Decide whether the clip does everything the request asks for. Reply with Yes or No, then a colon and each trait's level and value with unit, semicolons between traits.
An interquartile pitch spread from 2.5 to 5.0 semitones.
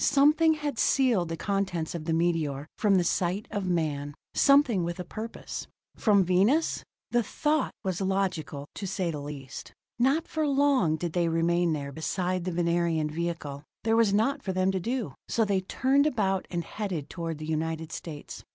No: wide, 5.4 semitones